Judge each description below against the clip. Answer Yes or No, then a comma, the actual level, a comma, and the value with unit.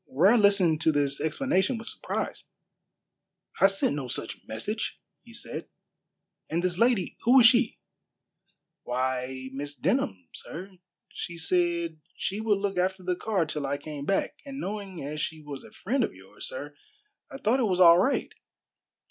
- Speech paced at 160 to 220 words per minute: Yes, average, 165 wpm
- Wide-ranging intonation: Yes, wide, 5.8 semitones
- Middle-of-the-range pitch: Yes, medium, 180 Hz